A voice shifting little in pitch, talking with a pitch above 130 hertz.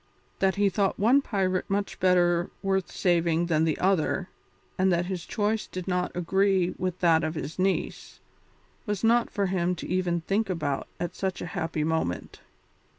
Yes: narrow, 2.3 semitones; medium, 185 Hz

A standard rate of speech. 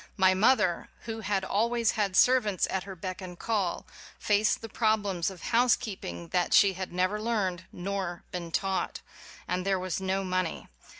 Yes: average, 170 wpm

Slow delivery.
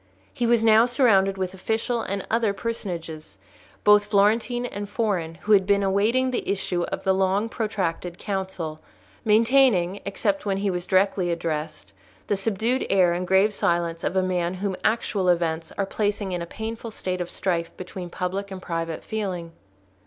No: average, 165 wpm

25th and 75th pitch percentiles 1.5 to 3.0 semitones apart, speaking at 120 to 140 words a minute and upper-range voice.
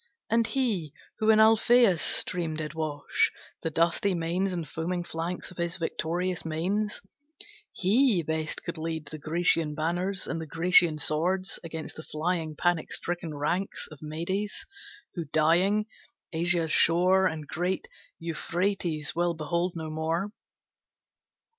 No: average, 2.7 semitones; slow, 135 wpm; medium, 170 Hz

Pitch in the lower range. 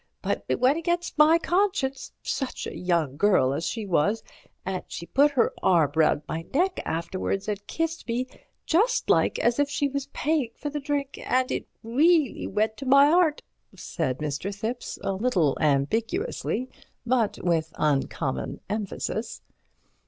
No: high, 230 Hz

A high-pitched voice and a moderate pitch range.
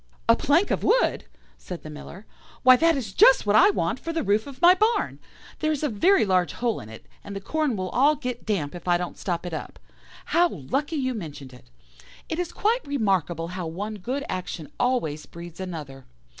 No: high, 210 Hz; wide, 8.7 semitones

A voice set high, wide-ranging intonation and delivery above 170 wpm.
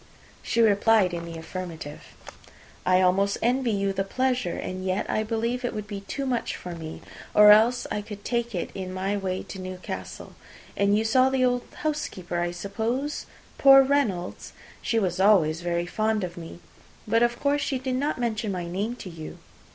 No: high, 205 Hz; average, 4.7 semitones; average, 185 wpm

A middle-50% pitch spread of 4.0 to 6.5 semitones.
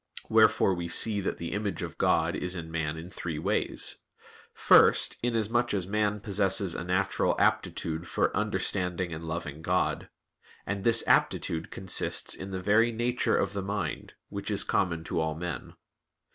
No: average, 3.5 semitones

